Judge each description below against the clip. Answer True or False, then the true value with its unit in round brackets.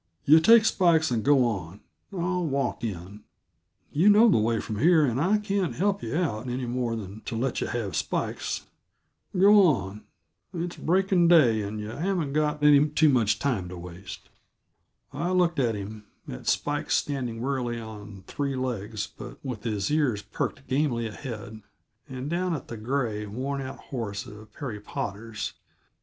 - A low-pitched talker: True (125 Hz)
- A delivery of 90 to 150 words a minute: False (170 wpm)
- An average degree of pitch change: False (6.5 semitones)